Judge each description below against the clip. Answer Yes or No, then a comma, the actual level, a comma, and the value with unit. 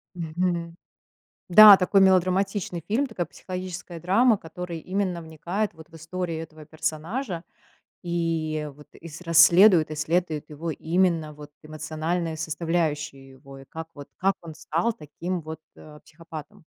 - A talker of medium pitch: Yes, medium, 165 Hz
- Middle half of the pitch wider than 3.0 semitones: No, average, 2.7 semitones